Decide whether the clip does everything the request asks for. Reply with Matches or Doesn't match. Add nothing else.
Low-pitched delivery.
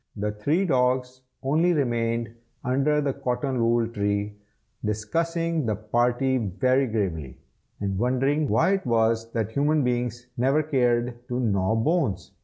Matches